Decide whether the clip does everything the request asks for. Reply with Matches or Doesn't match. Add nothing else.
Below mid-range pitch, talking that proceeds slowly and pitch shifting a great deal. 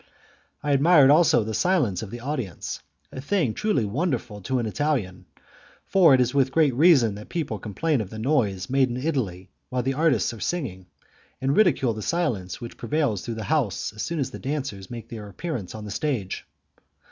Doesn't match